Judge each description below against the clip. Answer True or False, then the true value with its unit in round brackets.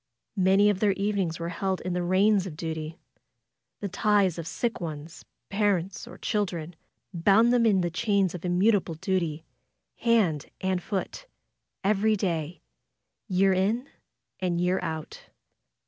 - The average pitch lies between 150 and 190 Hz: True (185 Hz)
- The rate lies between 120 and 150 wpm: True (140 wpm)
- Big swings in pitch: False (3.2 semitones)